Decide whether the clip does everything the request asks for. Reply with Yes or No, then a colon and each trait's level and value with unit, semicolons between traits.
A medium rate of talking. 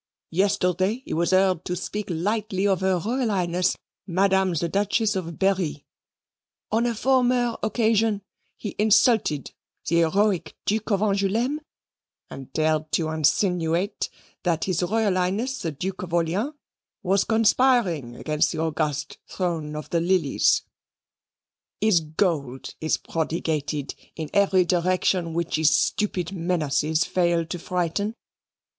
No: slow, 125 wpm